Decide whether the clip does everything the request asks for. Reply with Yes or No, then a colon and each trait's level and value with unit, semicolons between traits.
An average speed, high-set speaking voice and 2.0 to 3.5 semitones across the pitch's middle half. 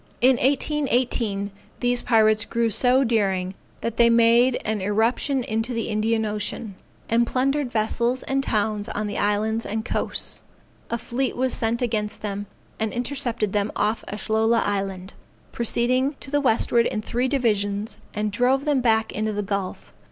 Yes: average, 155 wpm; high, 225 Hz; average, 2.8 semitones